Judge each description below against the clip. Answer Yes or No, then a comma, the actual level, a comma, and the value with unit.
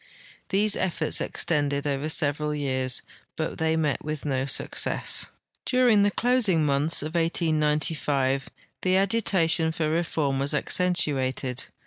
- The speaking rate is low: Yes, slow, 120 wpm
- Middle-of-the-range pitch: Yes, medium, 155 Hz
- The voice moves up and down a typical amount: Yes, average, 3.5 semitones